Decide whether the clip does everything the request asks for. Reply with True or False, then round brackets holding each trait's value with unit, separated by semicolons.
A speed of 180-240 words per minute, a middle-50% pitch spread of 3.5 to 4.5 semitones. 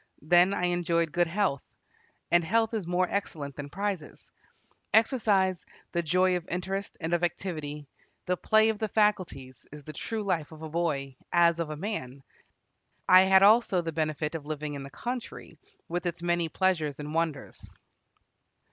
False (165 wpm; 3.8 semitones)